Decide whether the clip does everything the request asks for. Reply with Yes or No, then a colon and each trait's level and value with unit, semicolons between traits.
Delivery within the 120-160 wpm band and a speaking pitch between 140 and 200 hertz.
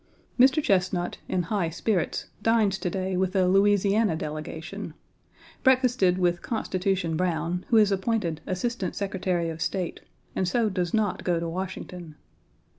Yes: average, 140 wpm; medium, 185 Hz